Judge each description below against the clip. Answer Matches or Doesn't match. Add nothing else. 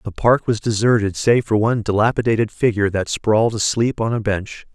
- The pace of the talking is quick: Doesn't match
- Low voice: Matches